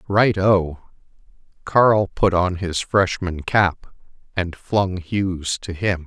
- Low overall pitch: Yes, very low, 95 Hz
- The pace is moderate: No, slow, 130 wpm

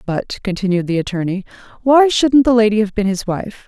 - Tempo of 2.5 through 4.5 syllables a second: No, 5.5 syllables/s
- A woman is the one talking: Yes, female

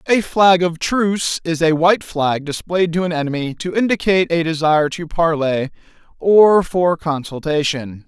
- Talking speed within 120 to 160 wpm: Yes, average, 155 wpm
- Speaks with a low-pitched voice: No, medium, 165 Hz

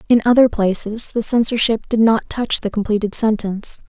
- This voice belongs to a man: No, female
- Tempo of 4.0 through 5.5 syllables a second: Yes, 5.3 syllables/s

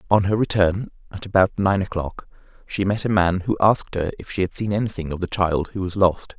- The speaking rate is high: Yes, fast, 235 wpm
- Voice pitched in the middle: No, very low, 95 Hz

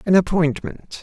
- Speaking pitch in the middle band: Yes, medium, 175 Hz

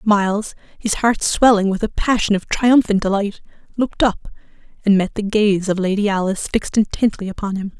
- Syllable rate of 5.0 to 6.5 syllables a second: Yes, 5.5 syllables/s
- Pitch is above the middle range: Yes, high, 205 Hz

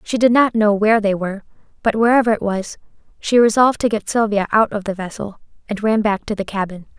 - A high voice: Yes, high, 215 Hz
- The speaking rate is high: Yes, fast, 225 wpm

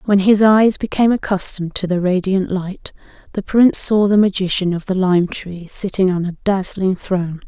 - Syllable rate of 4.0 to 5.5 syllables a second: Yes, 5.1 syllables/s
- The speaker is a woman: Yes, female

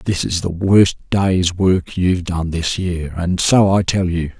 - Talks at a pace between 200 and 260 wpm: Yes, fast, 205 wpm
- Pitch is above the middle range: No, very low, 90 Hz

